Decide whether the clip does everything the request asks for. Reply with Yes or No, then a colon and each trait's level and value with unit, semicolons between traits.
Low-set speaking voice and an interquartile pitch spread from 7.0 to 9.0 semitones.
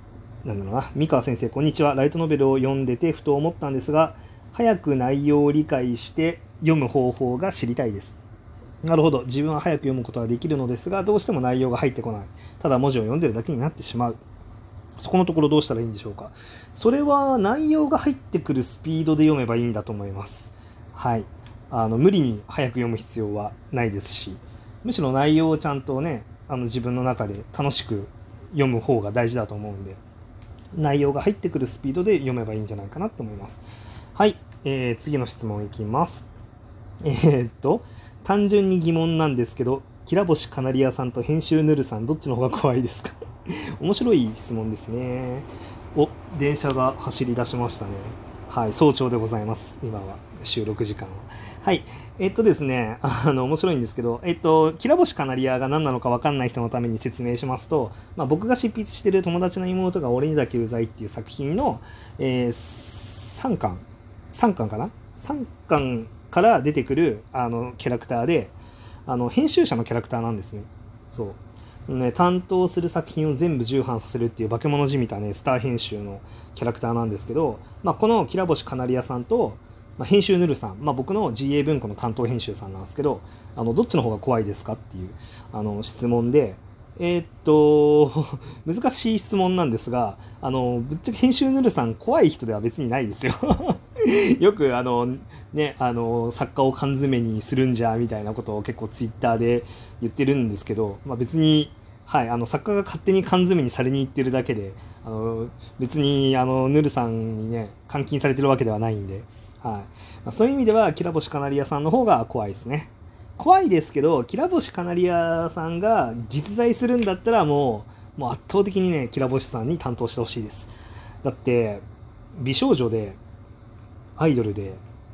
No: low, 125 Hz; wide, 5.4 semitones